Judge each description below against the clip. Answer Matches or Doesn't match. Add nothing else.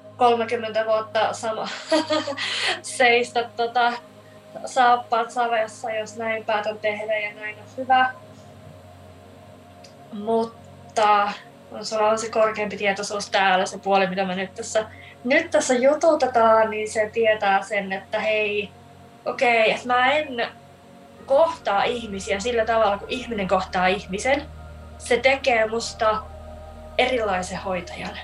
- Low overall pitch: Doesn't match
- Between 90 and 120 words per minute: Matches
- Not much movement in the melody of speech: Doesn't match